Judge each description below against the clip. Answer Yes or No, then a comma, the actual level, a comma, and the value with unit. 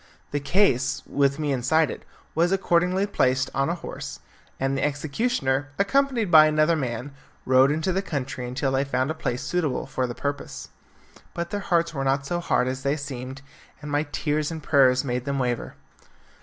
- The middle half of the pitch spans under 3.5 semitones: No, average, 4.0 semitones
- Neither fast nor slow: Yes, average, 185 wpm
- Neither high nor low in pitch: Yes, medium, 145 Hz